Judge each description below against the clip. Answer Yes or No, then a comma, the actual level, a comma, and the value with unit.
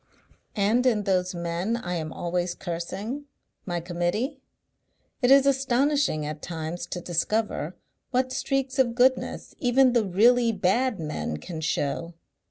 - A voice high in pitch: Yes, high, 205 Hz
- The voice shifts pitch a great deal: Yes, wide, 6.6 semitones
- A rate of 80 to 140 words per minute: Yes, slow, 135 wpm